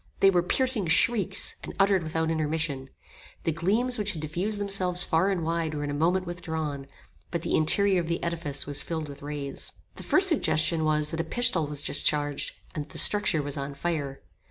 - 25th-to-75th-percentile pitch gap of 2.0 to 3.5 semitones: No, average, 4.0 semitones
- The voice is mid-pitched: Yes, medium, 165 Hz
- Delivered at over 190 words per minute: Yes, average, 200 wpm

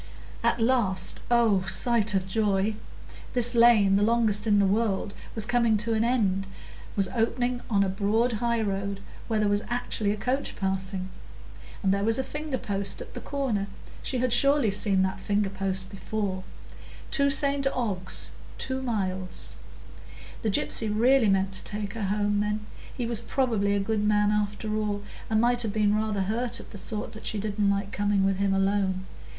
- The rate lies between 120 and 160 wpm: No, average, 170 wpm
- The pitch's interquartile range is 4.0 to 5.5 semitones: No, average, 2.9 semitones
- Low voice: No, high, 210 Hz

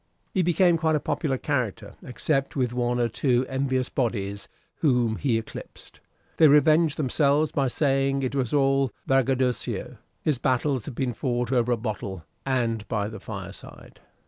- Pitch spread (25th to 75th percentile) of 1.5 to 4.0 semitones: Yes, average, 2.8 semitones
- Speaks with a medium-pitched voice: No, low, 130 Hz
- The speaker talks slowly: No, average, 155 wpm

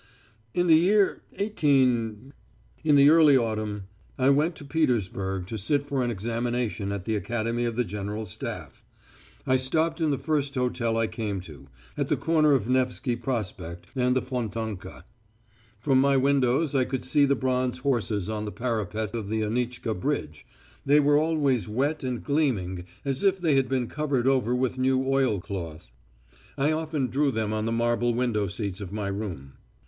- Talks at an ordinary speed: Yes, average, 175 wpm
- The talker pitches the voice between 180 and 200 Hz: No, low, 125 Hz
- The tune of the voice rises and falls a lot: No, average, 4.4 semitones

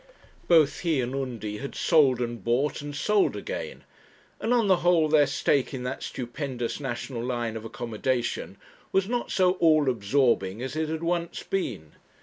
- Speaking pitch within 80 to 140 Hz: Yes, low, 135 Hz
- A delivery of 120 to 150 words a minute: No, average, 165 wpm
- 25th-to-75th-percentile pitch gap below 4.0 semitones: No, average, 5.1 semitones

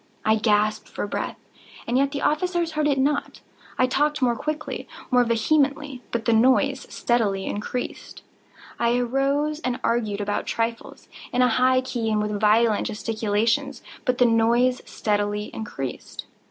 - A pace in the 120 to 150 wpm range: Yes, average, 140 wpm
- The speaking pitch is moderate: No, high, 240 Hz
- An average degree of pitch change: Yes, average, 3.9 semitones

